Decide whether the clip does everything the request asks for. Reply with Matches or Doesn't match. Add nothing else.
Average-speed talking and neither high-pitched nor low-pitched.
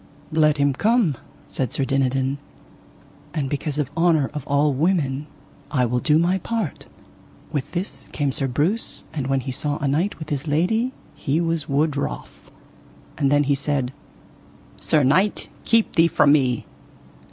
Matches